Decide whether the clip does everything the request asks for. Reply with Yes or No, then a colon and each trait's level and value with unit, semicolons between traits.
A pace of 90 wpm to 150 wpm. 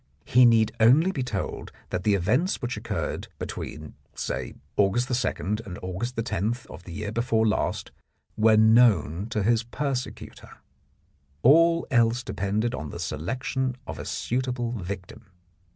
Yes: average, 140 wpm